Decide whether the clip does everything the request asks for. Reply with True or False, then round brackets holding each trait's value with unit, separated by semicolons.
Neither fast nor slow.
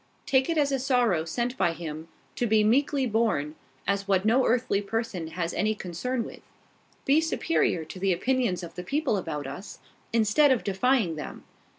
True (180 wpm)